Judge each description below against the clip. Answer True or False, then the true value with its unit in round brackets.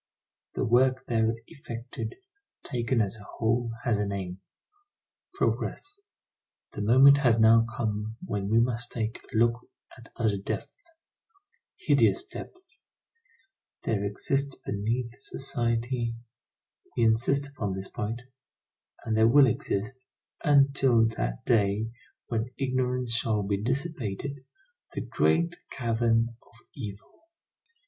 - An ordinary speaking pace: False (115 wpm)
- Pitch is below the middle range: True (115 Hz)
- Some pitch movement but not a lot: True (3.0 semitones)